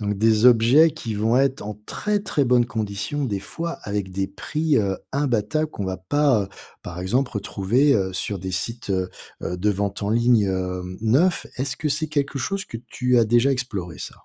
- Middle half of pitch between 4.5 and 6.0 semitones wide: Yes, wide, 5.6 semitones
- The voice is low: Yes, low, 115 Hz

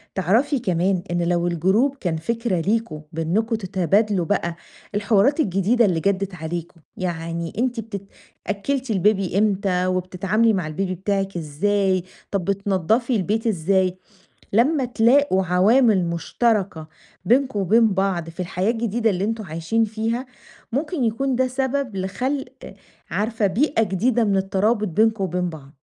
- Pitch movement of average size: Yes, average, 4.0 semitones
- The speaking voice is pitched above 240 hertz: No, high, 200 Hz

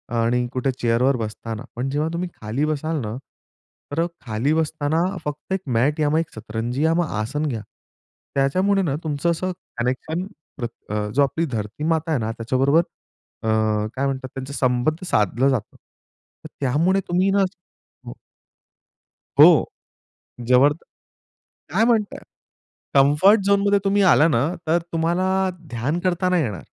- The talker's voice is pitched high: No, medium, 145 Hz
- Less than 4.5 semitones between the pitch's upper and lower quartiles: No, wide, 5.6 semitones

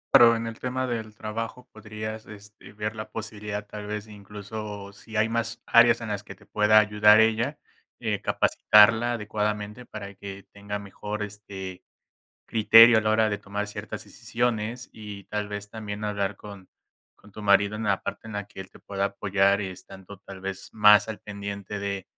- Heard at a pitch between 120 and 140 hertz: No, low, 105 Hz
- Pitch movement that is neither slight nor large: No, narrow, 1.5 semitones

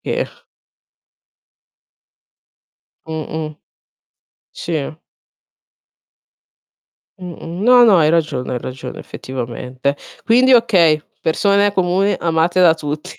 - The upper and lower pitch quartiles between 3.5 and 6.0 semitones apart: Yes, average, 4.2 semitones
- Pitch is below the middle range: No, medium, 165 Hz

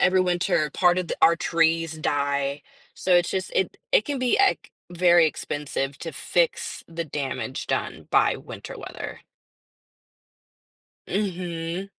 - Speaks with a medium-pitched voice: Yes, medium, 170 Hz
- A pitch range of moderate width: Yes, average, 3.5 semitones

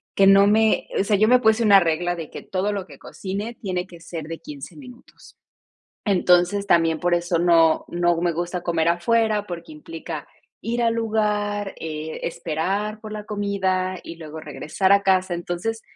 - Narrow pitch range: No, average, 3.5 semitones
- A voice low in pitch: No, high, 190 Hz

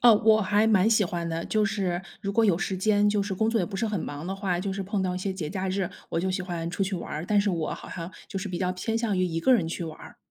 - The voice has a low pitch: No, high, 190 Hz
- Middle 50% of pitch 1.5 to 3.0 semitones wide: Yes, average, 2.7 semitones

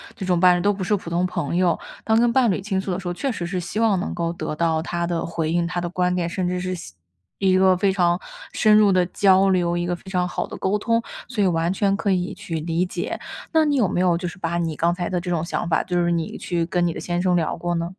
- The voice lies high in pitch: No, medium, 180 Hz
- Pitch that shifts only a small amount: Yes, narrow, 1.9 semitones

